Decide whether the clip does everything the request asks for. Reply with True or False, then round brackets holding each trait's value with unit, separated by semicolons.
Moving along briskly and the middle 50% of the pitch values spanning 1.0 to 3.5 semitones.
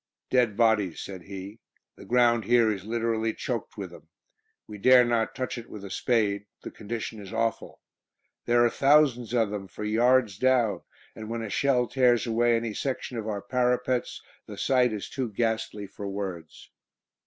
False (175 wpm; 2.9 semitones)